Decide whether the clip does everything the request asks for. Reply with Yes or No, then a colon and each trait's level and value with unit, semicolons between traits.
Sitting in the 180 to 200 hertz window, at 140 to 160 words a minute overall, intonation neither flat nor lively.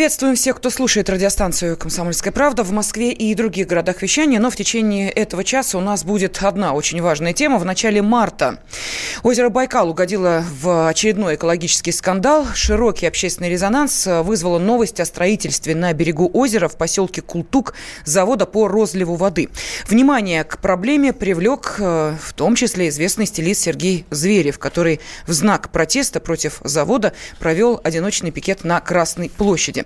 Yes: high, 190 Hz; average, 150 wpm; average, 4.7 semitones